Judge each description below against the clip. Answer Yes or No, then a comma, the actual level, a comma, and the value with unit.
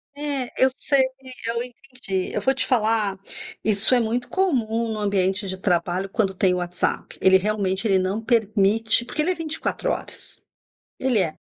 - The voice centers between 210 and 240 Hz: Yes, high, 215 Hz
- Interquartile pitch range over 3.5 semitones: Yes, average, 4.5 semitones